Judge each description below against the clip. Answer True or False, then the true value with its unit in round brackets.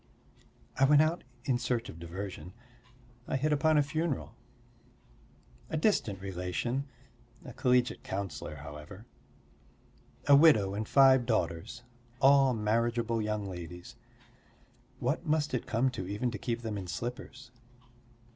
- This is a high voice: False (115 Hz)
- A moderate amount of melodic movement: False (5.7 semitones)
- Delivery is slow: True (125 wpm)